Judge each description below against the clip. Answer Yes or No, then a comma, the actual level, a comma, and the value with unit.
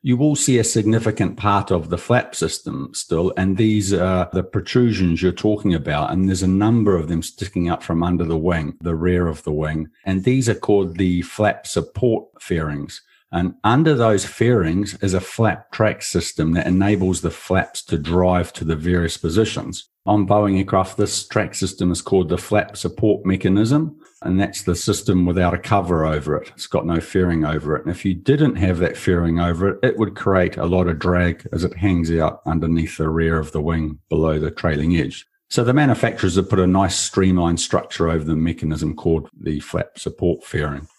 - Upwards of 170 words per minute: Yes, average, 200 wpm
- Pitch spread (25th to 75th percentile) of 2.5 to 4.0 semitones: Yes, average, 3.5 semitones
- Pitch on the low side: Yes, very low, 90 Hz